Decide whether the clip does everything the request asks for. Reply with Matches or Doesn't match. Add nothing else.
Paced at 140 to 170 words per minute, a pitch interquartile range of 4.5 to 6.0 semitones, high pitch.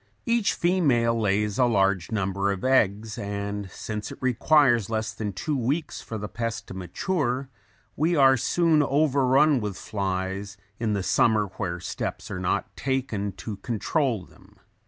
Doesn't match